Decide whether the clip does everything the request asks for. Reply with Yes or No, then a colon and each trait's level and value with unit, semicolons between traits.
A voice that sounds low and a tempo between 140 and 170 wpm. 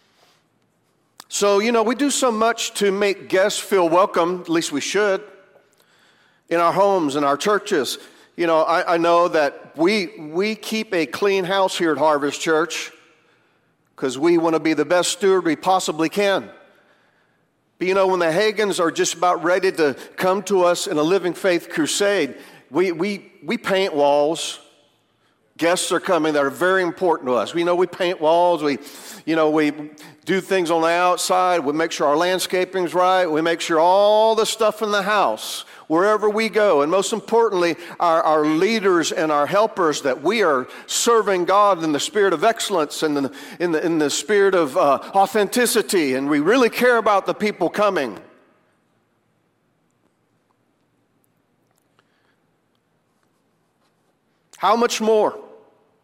No: medium, 185 Hz; average, 165 wpm